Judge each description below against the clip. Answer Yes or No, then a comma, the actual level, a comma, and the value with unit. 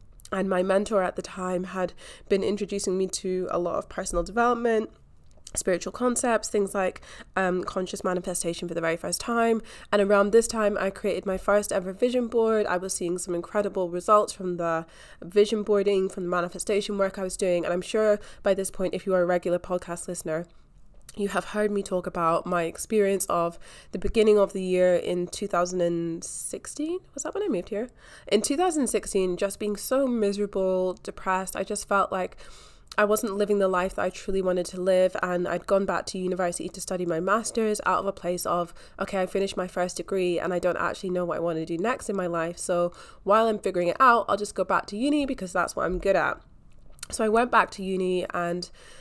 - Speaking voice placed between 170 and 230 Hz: Yes, high, 190 Hz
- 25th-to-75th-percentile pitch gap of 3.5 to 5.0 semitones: No, narrow, 2.5 semitones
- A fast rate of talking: Yes, fast, 210 wpm